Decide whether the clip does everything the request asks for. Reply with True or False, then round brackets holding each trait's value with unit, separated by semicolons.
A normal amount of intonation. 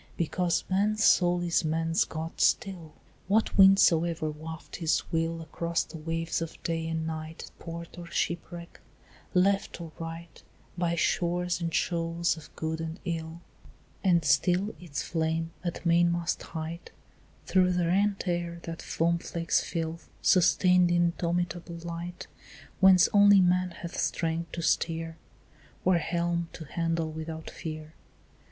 False (1.4 semitones)